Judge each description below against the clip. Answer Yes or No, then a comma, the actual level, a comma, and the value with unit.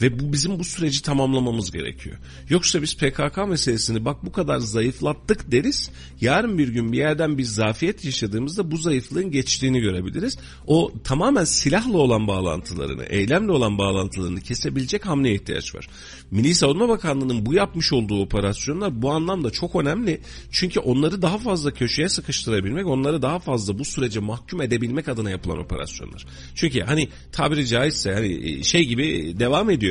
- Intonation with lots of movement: Yes, wide, 7.1 semitones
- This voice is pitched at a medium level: No, low, 130 Hz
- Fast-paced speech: Yes, fast, 155 wpm